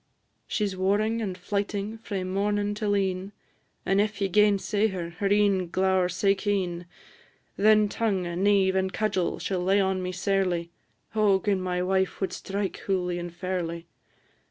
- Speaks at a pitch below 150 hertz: No, high, 195 Hz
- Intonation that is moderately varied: No, narrow, 1.9 semitones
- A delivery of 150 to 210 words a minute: Yes, average, 160 wpm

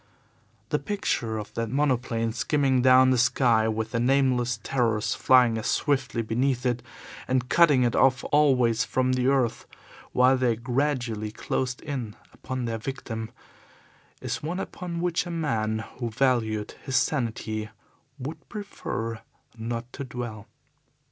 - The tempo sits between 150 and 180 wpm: No, average, 140 wpm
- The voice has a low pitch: Yes, low, 125 Hz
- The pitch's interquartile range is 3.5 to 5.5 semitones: No, average, 2.8 semitones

